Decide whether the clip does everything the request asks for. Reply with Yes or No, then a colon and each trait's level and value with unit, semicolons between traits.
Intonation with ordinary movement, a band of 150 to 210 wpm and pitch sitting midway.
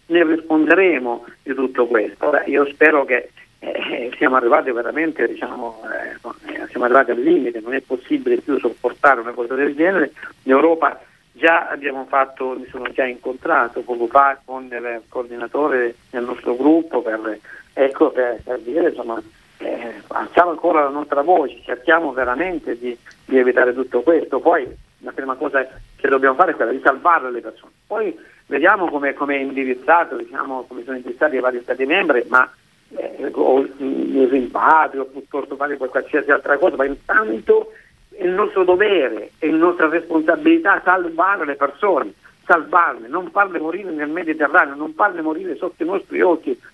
Yes: average, 4.9 semitones; average, 165 wpm; medium, 145 Hz